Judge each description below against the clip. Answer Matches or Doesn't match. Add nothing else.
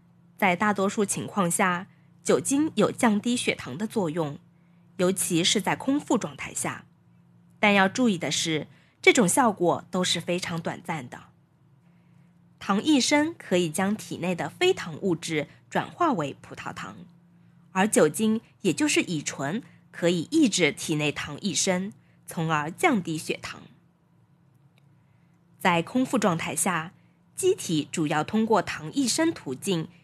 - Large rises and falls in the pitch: Doesn't match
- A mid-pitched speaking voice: Matches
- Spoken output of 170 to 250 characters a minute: Matches